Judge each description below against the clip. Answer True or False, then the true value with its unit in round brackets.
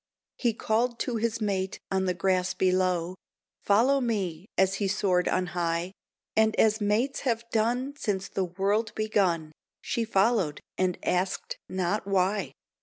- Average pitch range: True (3.2 semitones)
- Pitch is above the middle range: True (195 Hz)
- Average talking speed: True (145 wpm)